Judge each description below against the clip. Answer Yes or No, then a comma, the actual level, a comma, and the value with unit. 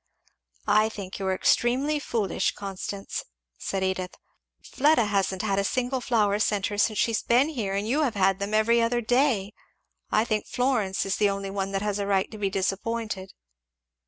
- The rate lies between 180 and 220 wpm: Yes, average, 190 wpm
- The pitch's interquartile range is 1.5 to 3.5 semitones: Yes, average, 3.2 semitones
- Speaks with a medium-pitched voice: No, high, 210 Hz